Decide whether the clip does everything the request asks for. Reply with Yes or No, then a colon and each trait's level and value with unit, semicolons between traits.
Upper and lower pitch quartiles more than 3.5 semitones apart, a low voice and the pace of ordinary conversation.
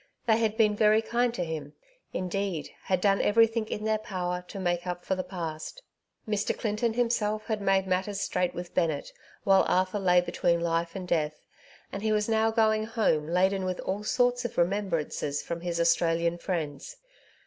No: average, 3.9 semitones; high, 190 Hz; average, 180 wpm